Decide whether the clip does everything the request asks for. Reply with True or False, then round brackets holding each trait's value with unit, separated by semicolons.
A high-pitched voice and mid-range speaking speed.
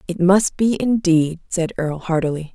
False (175 Hz; 165 wpm)